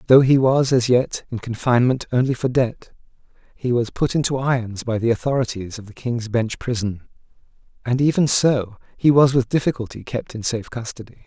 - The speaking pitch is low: Yes, low, 125 Hz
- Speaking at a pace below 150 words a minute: No, average, 180 wpm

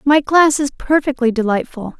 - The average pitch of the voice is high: Yes, very high, 270 Hz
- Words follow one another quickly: No, average, 150 wpm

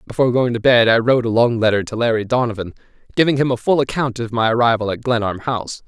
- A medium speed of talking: No, fast, 235 wpm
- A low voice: Yes, low, 120 Hz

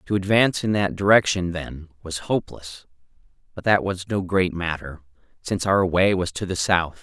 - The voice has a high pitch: No, very low, 90 Hz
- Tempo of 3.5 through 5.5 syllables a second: Yes, 5.1 syllables/s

